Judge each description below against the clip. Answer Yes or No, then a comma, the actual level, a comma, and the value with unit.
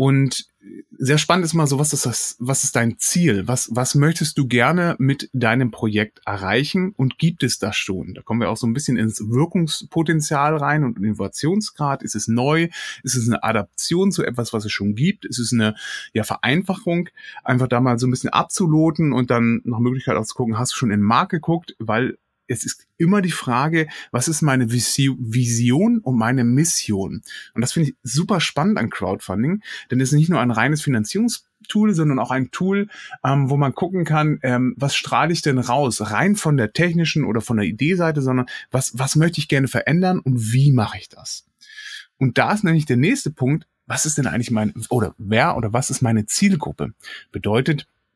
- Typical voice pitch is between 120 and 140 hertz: Yes, low, 135 Hz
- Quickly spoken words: Yes, fast, 200 wpm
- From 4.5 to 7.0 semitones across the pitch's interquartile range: Yes, wide, 5.5 semitones